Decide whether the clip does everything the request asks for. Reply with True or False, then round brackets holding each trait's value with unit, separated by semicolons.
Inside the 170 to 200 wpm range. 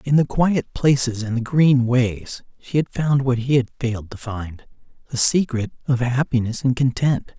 True (180 wpm)